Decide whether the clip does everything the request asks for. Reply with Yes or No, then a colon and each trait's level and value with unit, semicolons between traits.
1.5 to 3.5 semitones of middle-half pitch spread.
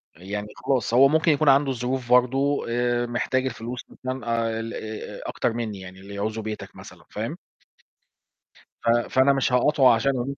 Yes: average, 2.9 semitones